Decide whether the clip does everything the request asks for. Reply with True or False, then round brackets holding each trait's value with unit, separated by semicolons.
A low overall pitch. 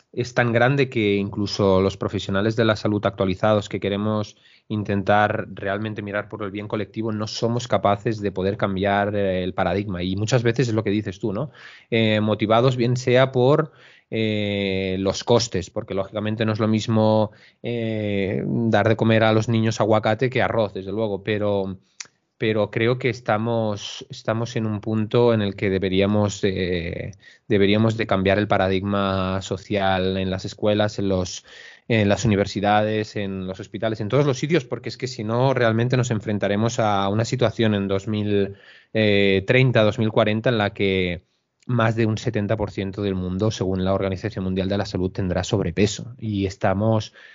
True (105 Hz)